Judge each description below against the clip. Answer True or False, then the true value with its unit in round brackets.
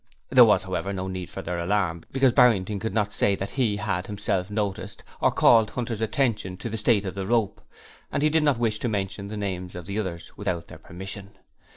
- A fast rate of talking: True (220 wpm)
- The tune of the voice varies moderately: True (3.0 semitones)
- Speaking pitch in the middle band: False (100 Hz)